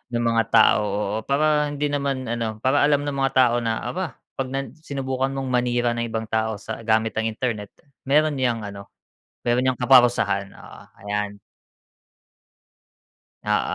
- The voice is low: Yes, low, 120 Hz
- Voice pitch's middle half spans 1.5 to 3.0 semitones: No, average, 3.5 semitones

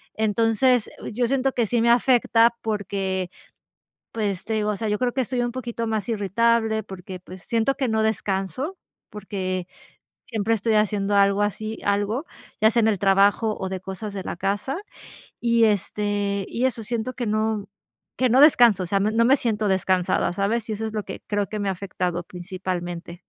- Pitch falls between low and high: No, high, 210 Hz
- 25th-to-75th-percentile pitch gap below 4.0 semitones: Yes, average, 2.9 semitones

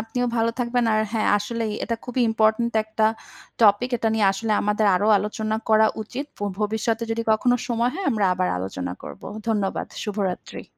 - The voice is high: Yes, high, 220 Hz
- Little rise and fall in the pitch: Yes, narrow, 1.9 semitones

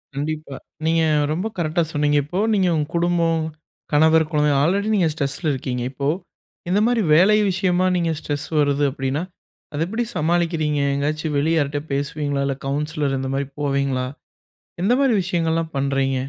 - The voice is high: No, medium, 155 Hz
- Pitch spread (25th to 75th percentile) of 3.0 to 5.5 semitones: Yes, average, 3.4 semitones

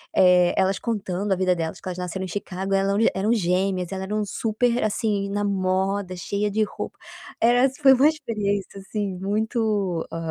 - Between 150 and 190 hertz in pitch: No, high, 200 Hz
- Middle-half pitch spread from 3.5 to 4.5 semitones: No, narrow, 2.4 semitones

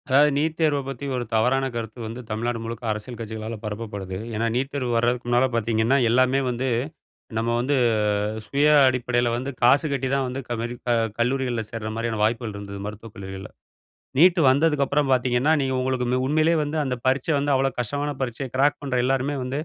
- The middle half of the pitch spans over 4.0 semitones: No, average, 3.0 semitones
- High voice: No, low, 125 Hz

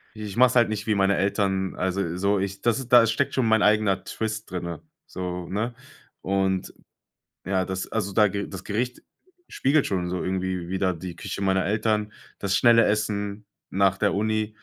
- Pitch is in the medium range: No, low, 100 Hz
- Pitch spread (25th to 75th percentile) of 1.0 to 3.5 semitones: Yes, narrow, 2.5 semitones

